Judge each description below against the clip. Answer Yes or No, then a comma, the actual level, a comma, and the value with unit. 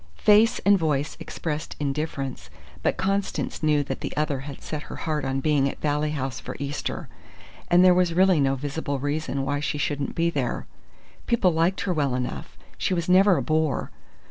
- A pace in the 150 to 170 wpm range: No, average, 185 wpm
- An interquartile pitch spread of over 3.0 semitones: Yes, average, 3.8 semitones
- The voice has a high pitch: No, medium, 150 Hz